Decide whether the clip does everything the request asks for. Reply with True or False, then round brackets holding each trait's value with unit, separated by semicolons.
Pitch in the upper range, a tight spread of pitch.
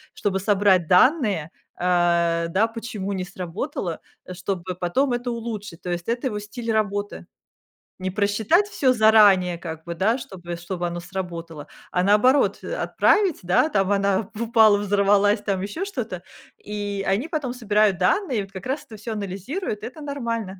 False (205 Hz; 4.2 semitones)